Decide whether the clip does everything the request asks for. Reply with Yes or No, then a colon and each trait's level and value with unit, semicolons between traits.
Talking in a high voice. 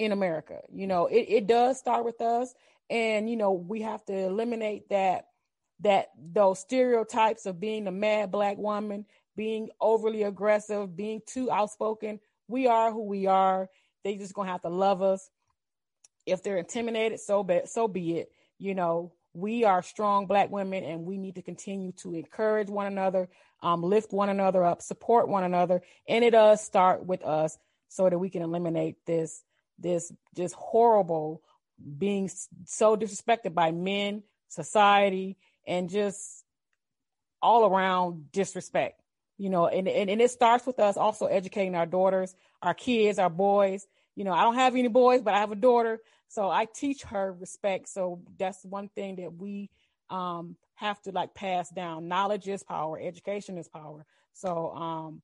Yes: high, 195 Hz